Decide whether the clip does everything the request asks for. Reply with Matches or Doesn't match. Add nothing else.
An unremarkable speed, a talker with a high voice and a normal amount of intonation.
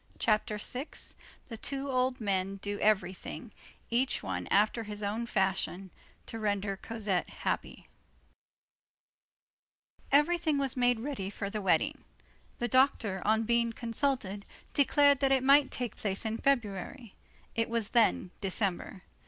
Doesn't match